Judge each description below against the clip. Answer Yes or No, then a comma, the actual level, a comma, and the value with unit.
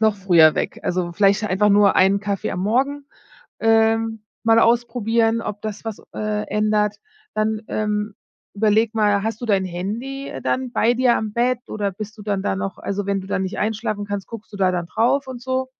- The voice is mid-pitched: No, high, 215 Hz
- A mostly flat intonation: Yes, narrow, 2.3 semitones